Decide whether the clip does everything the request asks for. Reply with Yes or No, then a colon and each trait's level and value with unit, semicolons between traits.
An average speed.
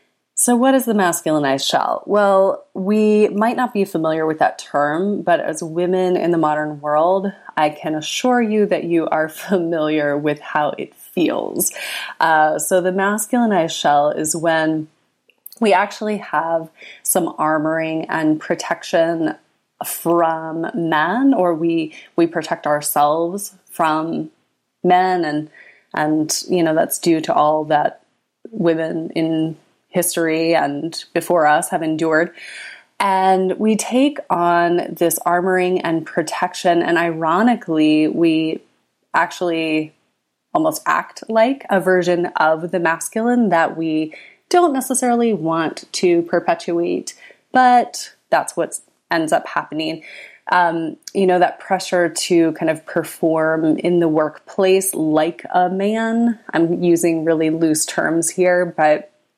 No: slow, 130 wpm